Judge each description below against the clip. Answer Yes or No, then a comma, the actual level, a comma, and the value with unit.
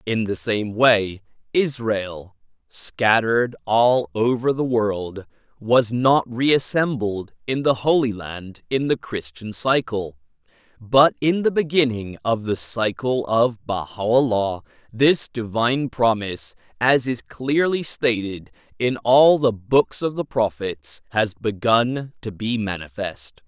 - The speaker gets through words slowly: Yes, slow, 125 wpm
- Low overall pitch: Yes, low, 115 Hz